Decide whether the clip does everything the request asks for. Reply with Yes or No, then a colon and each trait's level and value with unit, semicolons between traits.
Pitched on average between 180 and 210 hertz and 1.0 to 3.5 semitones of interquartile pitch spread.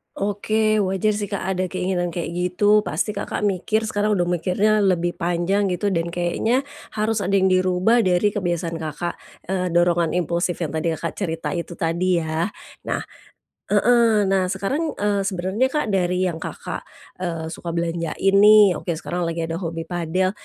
Yes: medium, 185 Hz; average, 3.0 semitones